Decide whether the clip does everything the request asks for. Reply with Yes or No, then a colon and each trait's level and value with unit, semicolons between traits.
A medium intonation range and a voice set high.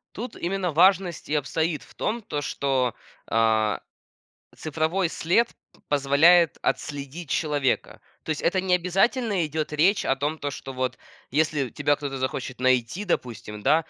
No: average, 4.7 semitones; medium, 150 Hz